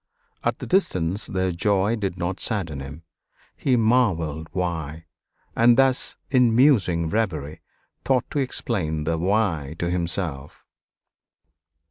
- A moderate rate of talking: No, slow, 120 wpm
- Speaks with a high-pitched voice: No, very low, 90 Hz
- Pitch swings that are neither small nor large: No, wide, 5.9 semitones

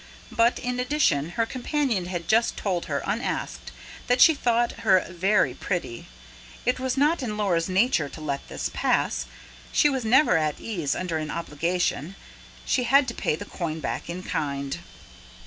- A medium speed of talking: Yes, average, 165 wpm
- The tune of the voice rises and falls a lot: Yes, wide, 7.0 semitones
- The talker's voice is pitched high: Yes, high, 195 Hz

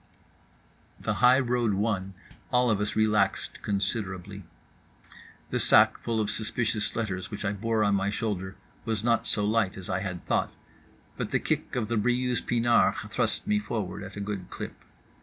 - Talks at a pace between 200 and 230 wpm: No, average, 165 wpm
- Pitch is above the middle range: No, low, 105 Hz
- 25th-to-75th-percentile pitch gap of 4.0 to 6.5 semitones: No, average, 2.8 semitones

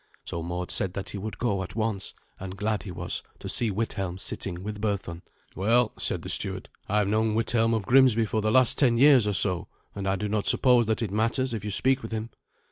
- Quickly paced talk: Yes, fast, 230 wpm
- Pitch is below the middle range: Yes, low, 105 Hz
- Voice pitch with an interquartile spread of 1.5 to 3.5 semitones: Yes, average, 2.9 semitones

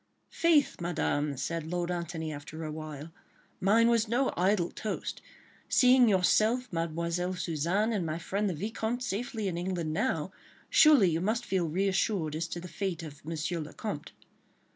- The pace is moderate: Yes, average, 160 wpm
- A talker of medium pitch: Yes, medium, 180 Hz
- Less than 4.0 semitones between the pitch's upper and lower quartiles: No, average, 4.8 semitones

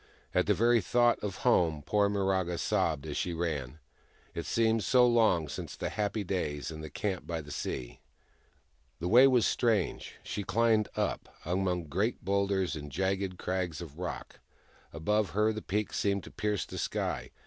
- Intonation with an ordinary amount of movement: Yes, average, 4.3 semitones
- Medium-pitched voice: No, very low, 95 Hz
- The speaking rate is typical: Yes, average, 170 wpm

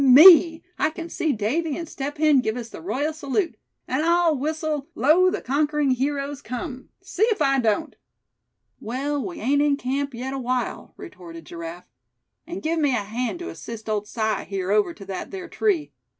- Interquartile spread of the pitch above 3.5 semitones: Yes, average, 5.2 semitones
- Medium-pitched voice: No, very high, 280 Hz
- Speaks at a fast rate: No, average, 180 wpm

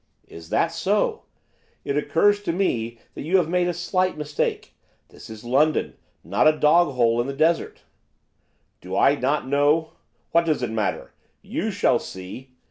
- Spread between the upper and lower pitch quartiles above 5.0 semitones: Yes, wide, 5.5 semitones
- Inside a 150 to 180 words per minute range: Yes, average, 165 wpm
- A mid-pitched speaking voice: Yes, medium, 150 Hz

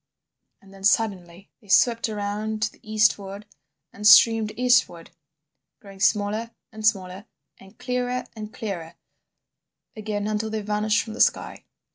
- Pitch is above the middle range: Yes, high, 210 Hz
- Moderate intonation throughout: No, narrow, 1.8 semitones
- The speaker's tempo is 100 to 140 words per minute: Yes, slow, 135 wpm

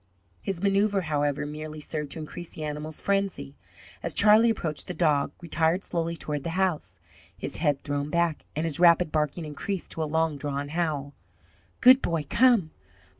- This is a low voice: No, medium, 160 Hz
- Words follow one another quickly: No, average, 170 wpm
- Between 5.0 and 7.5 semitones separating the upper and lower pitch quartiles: No, average, 3.1 semitones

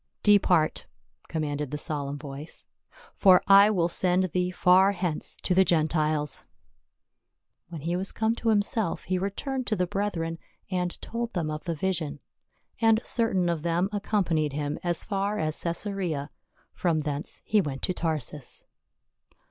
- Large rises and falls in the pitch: No, average, 4.2 semitones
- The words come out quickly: No, average, 150 wpm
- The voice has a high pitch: No, medium, 175 Hz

